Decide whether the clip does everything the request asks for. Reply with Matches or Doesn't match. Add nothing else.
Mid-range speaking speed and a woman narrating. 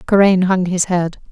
Matches